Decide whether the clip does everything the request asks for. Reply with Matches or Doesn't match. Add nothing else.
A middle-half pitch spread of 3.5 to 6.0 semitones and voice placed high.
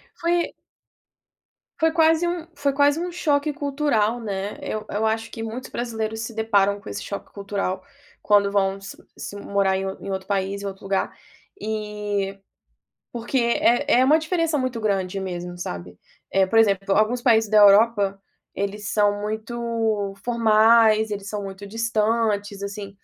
Doesn't match